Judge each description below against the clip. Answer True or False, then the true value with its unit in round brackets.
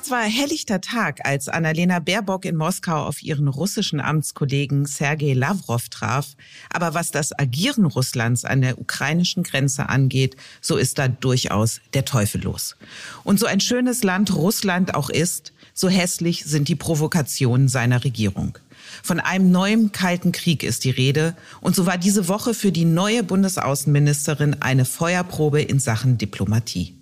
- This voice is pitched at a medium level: True (155 Hz)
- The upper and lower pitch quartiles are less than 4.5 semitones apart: False (5.5 semitones)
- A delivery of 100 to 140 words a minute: False (155 wpm)